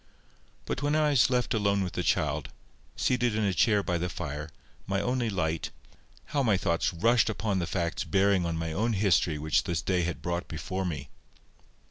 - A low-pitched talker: Yes, very low, 95 Hz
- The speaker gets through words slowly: No, average, 190 wpm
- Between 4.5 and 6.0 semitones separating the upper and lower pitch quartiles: Yes, average, 4.8 semitones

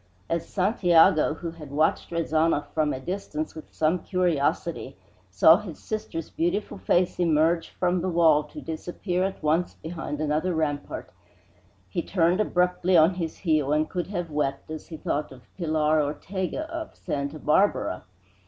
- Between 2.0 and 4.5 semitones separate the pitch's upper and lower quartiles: Yes, average, 2.8 semitones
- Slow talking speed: No, average, 155 wpm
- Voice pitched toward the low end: No, medium, 165 Hz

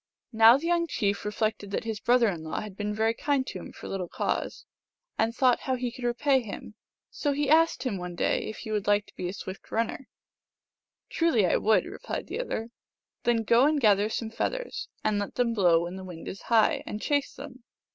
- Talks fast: Yes, fast, 225 wpm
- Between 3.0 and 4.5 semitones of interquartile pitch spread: Yes, average, 4.1 semitones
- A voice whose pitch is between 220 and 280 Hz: Yes, high, 225 Hz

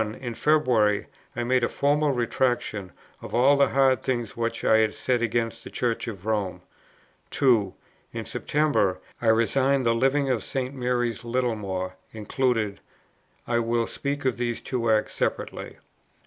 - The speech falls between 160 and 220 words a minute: No, average, 150 wpm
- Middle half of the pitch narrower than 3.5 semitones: Yes, average, 2.9 semitones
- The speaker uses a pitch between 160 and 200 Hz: No, low, 120 Hz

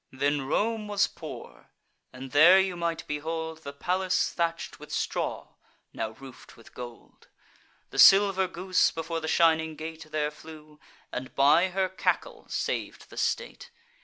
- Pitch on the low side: No, medium, 160 Hz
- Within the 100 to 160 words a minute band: Yes, average, 145 wpm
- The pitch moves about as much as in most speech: Yes, average, 3.8 semitones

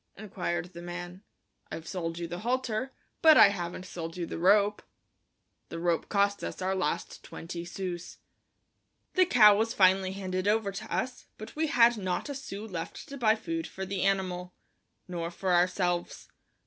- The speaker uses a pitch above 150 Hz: Yes, high, 190 Hz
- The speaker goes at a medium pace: Yes, average, 170 wpm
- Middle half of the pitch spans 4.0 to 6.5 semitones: No, average, 3.6 semitones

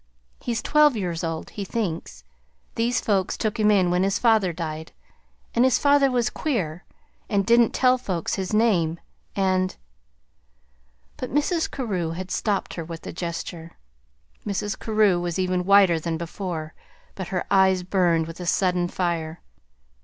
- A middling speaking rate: Yes, average, 155 wpm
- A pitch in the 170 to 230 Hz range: Yes, medium, 185 Hz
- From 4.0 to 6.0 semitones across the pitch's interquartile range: Yes, average, 4.4 semitones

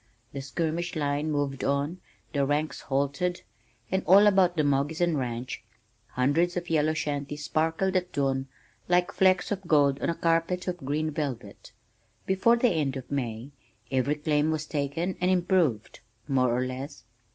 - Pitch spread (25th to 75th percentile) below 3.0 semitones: No, average, 4.0 semitones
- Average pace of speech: Yes, average, 155 wpm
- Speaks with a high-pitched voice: No, medium, 150 Hz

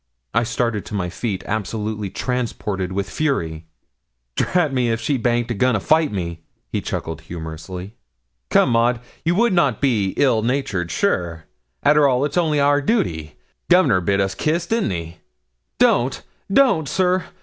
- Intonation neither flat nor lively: No, wide, 7.3 semitones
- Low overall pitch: Yes, low, 115 Hz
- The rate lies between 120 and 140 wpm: No, average, 160 wpm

